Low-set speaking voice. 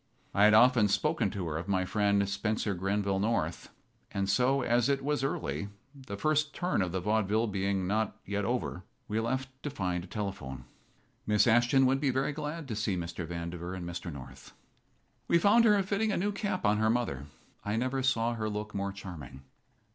Yes: low, 105 Hz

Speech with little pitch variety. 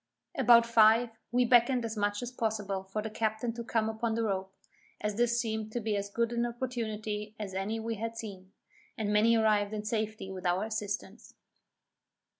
Yes: narrow, 1.9 semitones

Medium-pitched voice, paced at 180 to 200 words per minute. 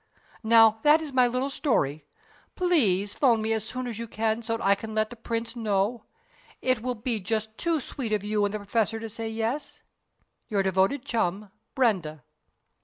No: high, 225 Hz; average, 185 wpm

